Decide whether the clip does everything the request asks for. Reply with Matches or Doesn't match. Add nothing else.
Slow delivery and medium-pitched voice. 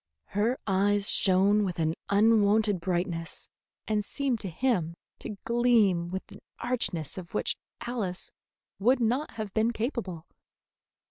Doesn't match